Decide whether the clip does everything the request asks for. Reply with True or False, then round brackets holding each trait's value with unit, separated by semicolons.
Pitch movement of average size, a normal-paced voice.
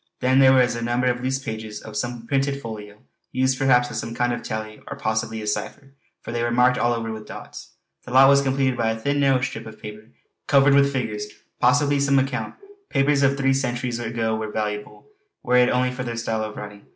False (3.2 semitones; 225 wpm)